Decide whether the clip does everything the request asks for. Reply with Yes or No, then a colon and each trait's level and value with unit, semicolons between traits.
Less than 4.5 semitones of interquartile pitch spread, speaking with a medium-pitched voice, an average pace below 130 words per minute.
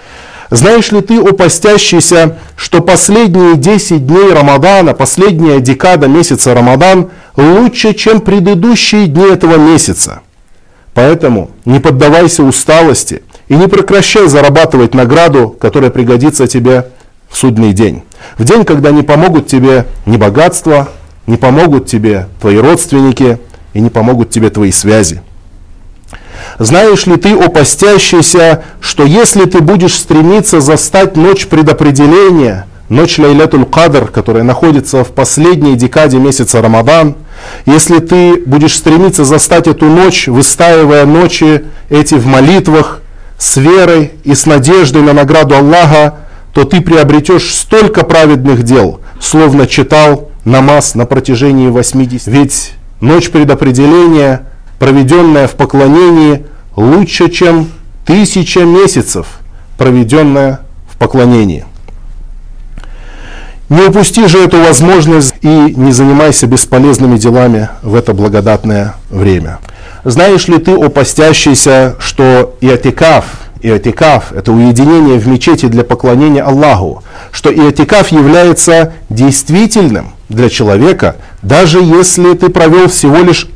No: wide, 5.5 semitones; medium, 145 Hz; average, 115 wpm